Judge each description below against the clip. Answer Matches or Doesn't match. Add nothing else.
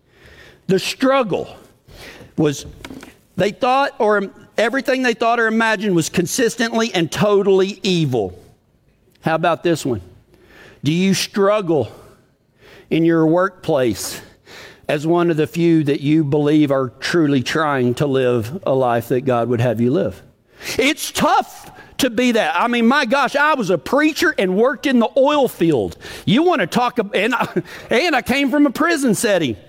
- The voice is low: Doesn't match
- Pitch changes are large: Matches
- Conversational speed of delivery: Matches